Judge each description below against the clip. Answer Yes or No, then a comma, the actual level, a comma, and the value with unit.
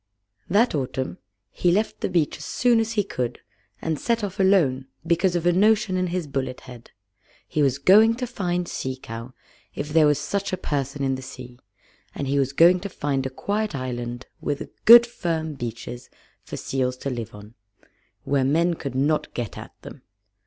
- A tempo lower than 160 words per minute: No, average, 190 wpm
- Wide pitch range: Yes, wide, 5.9 semitones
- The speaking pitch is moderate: Yes, medium, 150 Hz